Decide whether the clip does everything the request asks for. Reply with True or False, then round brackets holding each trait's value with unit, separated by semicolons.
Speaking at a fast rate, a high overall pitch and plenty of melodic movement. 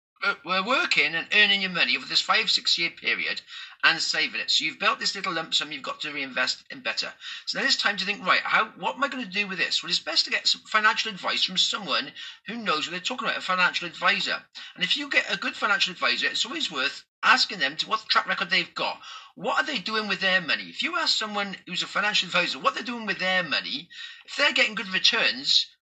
True (245 wpm; 215 Hz; 6.2 semitones)